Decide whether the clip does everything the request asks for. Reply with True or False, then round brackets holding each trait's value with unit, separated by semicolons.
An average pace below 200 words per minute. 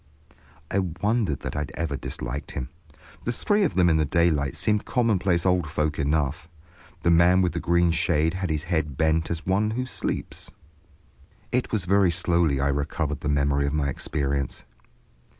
True (175 wpm)